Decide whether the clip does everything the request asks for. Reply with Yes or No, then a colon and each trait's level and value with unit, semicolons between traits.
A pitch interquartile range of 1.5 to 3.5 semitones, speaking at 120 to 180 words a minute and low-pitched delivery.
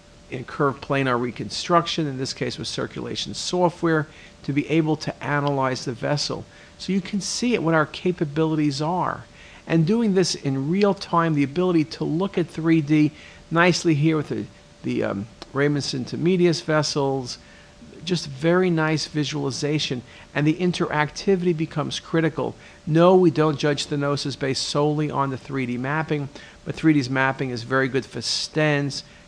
No: average, 3.2 semitones; average, 155 wpm; medium, 150 Hz